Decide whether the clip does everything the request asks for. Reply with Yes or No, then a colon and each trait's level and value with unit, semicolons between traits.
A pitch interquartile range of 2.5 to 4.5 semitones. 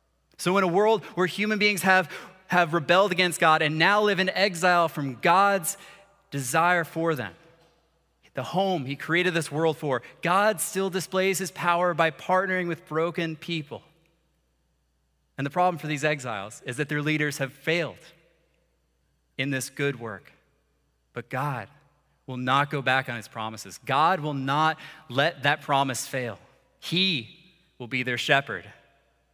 No: wide, 5.4 semitones